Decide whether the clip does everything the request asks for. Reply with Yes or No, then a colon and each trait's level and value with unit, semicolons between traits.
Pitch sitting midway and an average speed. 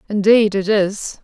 No: high, 205 Hz; average, 145 wpm